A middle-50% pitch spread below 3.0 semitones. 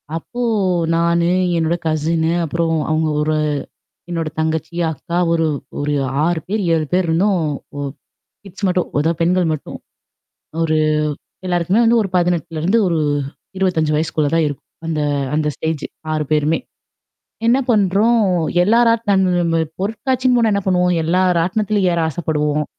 No: average, 3.3 semitones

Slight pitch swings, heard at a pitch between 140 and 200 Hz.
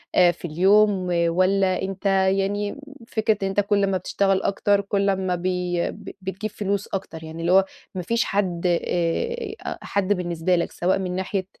Yes: narrow, 1.9 semitones; high, 190 Hz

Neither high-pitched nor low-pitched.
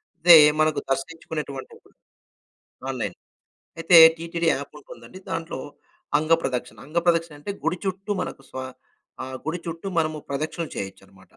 Yes: medium, 155 Hz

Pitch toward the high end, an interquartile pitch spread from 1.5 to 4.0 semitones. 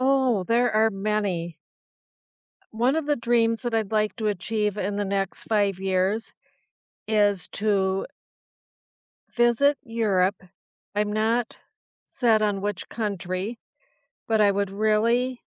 Yes: high, 215 Hz; narrow, 2.6 semitones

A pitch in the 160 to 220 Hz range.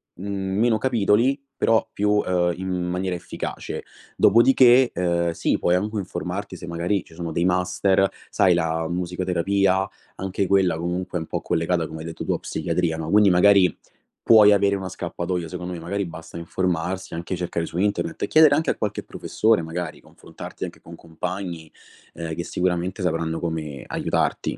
No: very low, 90 Hz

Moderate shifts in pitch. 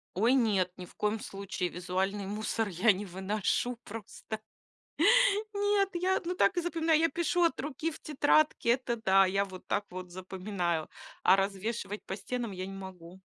No: wide, 6.0 semitones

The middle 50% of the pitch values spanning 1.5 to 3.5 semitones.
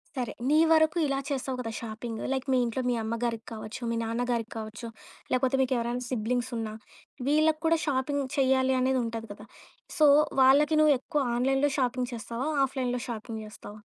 Yes: average, 2.8 semitones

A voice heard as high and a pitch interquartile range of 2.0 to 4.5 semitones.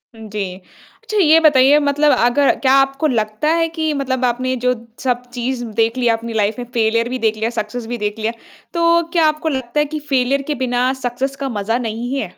Yes: very high, 250 Hz; average, 3.9 semitones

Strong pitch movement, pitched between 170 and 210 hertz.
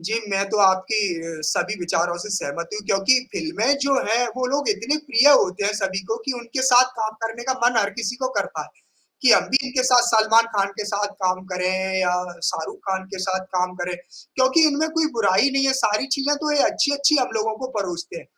No: wide, 5.8 semitones; high, 220 Hz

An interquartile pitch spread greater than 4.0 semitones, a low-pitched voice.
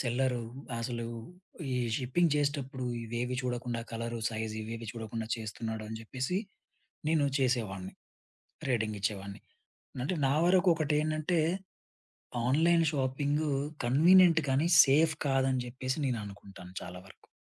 Yes: average, 4.6 semitones; low, 125 Hz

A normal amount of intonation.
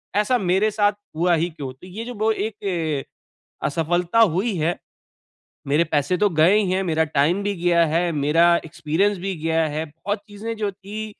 Yes: average, 4.1 semitones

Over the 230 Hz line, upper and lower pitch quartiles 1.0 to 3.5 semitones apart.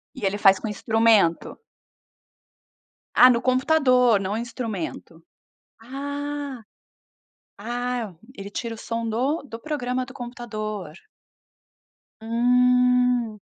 Yes: high, 240 Hz; average, 2.7 semitones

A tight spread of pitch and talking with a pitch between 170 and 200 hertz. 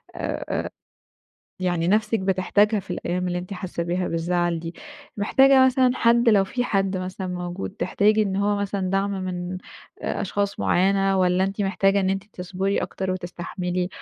Yes: narrow, 2.0 semitones; high, 190 Hz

